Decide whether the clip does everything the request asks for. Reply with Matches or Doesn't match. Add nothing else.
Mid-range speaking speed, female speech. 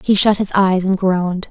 Doesn't match